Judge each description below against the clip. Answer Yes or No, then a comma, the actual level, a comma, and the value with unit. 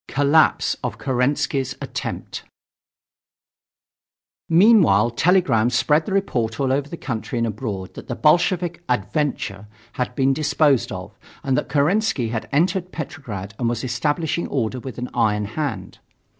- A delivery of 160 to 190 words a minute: No, slow, 135 wpm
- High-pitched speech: No, low, 135 Hz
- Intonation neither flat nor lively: Yes, average, 4.9 semitones